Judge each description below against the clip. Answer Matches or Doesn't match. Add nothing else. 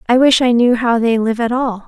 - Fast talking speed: Matches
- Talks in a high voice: Matches